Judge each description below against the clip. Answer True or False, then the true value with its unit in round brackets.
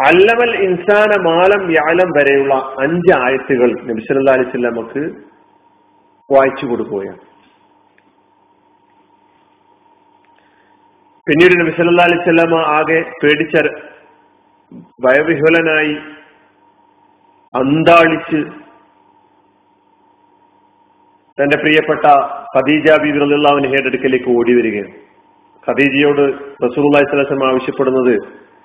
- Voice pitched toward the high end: False (170 Hz)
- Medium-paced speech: False (55 wpm)